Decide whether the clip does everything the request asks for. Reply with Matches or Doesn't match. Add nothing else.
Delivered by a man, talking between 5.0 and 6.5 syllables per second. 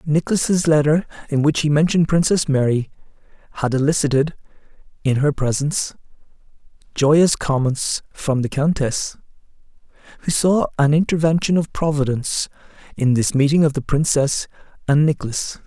Matches